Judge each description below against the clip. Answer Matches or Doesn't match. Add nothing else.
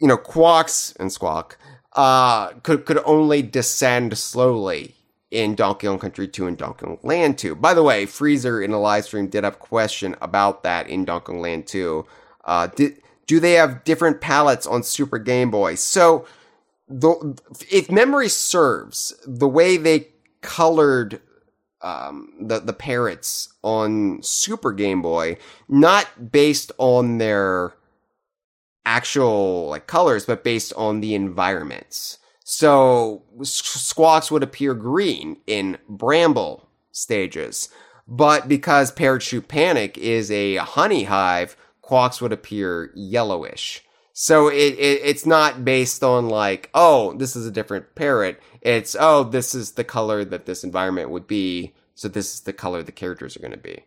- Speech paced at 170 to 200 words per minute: Doesn't match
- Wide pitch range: Matches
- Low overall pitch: Matches